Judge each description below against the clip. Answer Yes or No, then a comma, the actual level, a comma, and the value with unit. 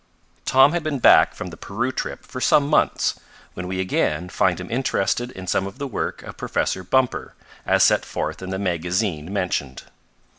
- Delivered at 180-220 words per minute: Yes, average, 185 wpm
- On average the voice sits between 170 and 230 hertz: No, very low, 95 Hz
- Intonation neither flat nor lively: No, wide, 6.2 semitones